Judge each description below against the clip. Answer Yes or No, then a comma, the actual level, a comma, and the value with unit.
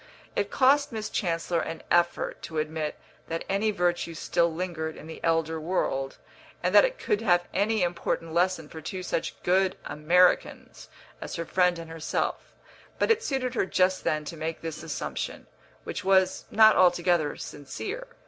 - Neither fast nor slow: Yes, average, 165 wpm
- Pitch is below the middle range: No, medium, 175 Hz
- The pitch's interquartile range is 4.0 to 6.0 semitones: No, average, 3.0 semitones